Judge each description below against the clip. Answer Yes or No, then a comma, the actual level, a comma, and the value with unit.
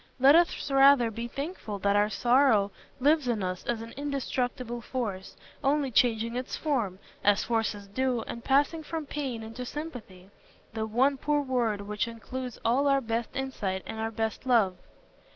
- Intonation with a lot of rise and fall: No, average, 3.8 semitones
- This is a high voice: Yes, high, 240 Hz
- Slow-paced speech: No, average, 160 wpm